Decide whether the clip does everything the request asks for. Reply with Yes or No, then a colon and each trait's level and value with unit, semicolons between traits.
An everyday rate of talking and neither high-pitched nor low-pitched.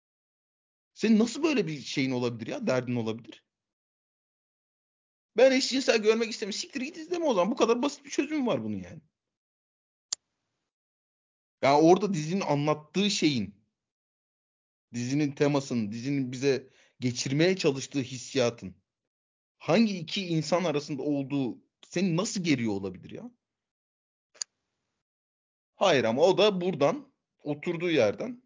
Yes: average, 120 wpm; medium, 155 Hz